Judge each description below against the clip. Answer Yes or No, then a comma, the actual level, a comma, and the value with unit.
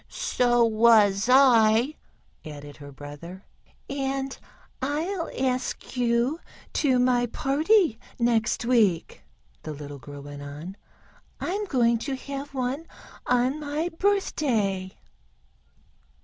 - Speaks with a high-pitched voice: Yes, high, 245 Hz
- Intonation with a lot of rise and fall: Yes, wide, 6.1 semitones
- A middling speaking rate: No, slow, 105 wpm